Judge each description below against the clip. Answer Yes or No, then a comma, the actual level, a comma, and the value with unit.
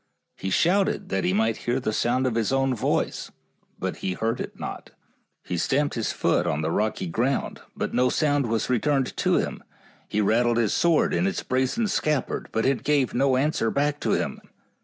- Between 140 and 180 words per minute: No, average, 195 wpm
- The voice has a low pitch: Yes, low, 125 Hz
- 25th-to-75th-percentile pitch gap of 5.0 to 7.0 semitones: No, average, 4.1 semitones